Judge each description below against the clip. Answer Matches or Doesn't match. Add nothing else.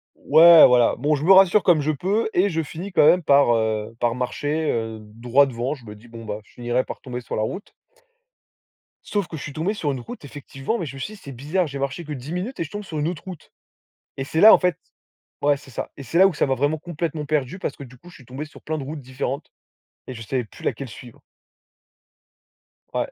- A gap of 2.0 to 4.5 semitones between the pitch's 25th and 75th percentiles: Doesn't match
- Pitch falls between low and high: Matches